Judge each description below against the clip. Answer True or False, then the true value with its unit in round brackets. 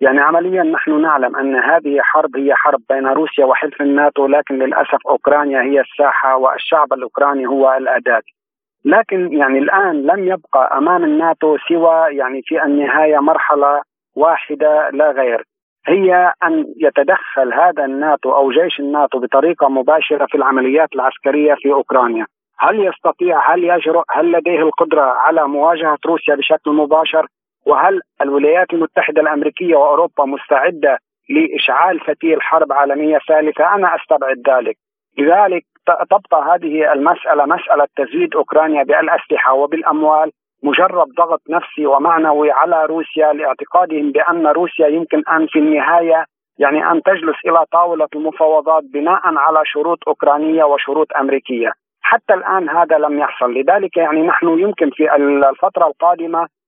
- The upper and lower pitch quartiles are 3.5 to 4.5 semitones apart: False (2.9 semitones)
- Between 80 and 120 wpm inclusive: False (130 wpm)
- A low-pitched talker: False (155 Hz)